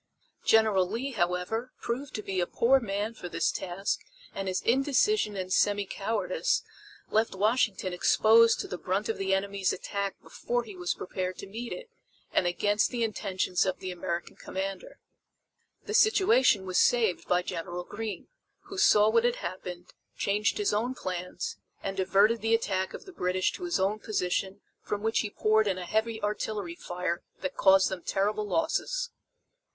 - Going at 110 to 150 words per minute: No, average, 170 wpm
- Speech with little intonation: No, average, 3.6 semitones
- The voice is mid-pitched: No, high, 205 Hz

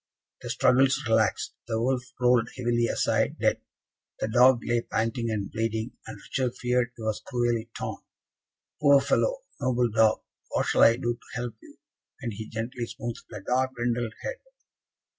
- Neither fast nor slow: Yes, average, 160 wpm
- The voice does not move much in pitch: Yes, narrow, 1.8 semitones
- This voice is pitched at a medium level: No, low, 120 Hz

